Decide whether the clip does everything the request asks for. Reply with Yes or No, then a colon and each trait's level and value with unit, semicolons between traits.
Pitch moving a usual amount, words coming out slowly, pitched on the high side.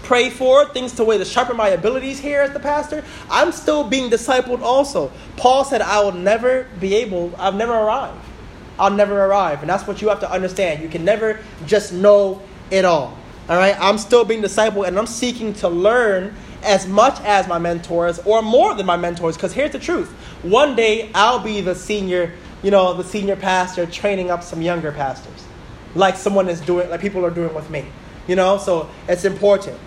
No: average, 3.8 semitones; fast, 205 wpm; high, 200 Hz